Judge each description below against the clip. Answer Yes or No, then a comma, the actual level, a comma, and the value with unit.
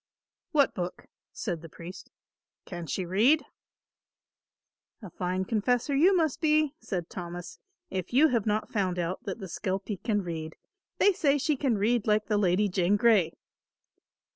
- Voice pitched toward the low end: No, high, 205 Hz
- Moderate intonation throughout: No, wide, 5.7 semitones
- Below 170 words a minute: Yes, average, 155 wpm